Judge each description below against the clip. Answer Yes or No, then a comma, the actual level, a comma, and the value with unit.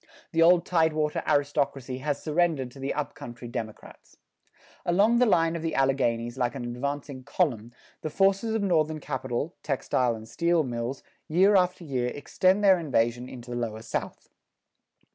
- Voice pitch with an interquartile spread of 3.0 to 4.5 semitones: No, wide, 5.6 semitones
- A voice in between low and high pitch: Yes, medium, 145 Hz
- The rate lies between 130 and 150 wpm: No, average, 160 wpm